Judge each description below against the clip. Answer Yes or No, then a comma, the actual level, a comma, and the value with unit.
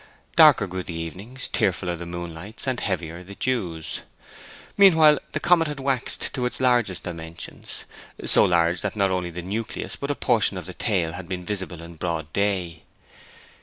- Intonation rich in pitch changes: Yes, wide, 6.1 semitones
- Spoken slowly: No, average, 170 wpm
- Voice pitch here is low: Yes, very low, 95 Hz